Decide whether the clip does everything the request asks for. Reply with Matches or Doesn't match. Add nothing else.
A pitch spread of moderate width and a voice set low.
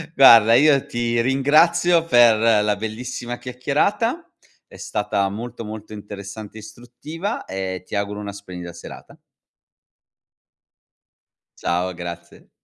Matches